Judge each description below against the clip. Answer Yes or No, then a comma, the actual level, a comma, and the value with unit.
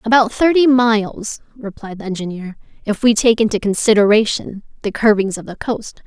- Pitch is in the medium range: No, high, 220 Hz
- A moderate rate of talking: Yes, average, 160 wpm